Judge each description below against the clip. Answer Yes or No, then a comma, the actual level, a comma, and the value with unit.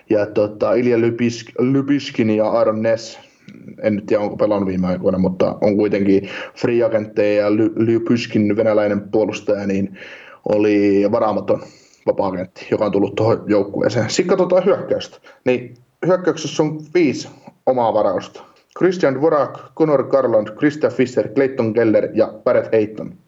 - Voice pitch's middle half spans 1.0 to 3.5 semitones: No, average, 3.9 semitones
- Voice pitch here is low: Yes, low, 115 Hz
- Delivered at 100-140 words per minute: Yes, average, 130 wpm